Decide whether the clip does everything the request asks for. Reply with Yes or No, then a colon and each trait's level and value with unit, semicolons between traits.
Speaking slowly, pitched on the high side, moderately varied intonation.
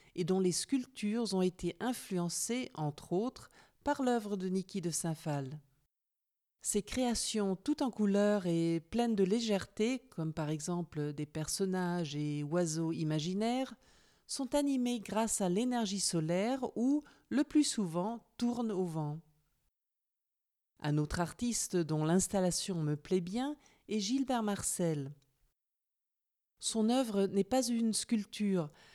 No: slow, 130 wpm; high, 195 Hz; wide, 5.9 semitones